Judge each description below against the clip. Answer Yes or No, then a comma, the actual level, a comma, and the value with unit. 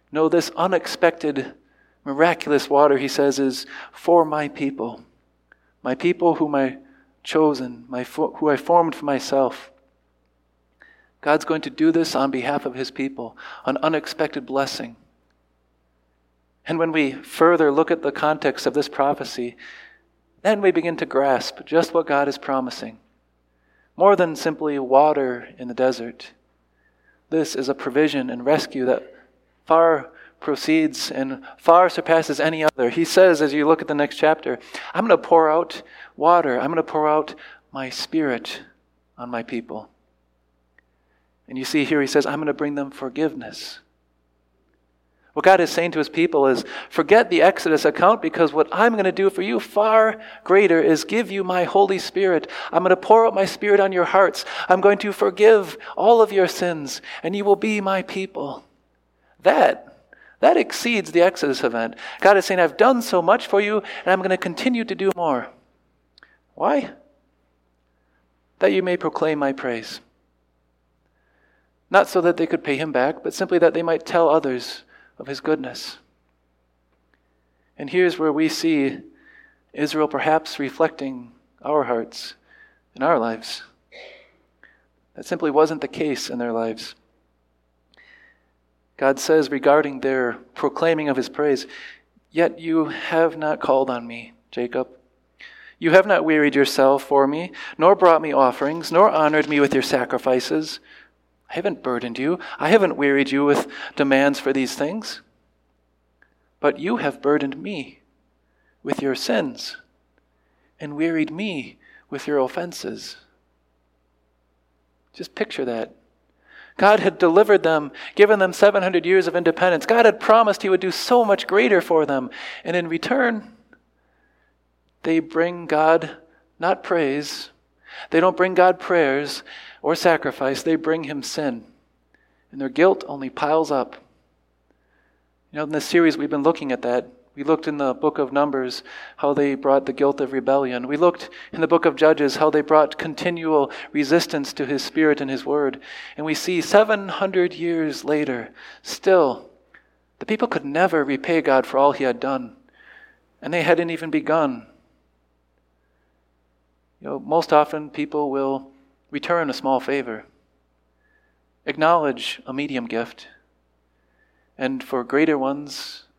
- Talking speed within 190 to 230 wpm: No, average, 155 wpm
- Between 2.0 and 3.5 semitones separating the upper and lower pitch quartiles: No, wide, 5.4 semitones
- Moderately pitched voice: Yes, medium, 145 Hz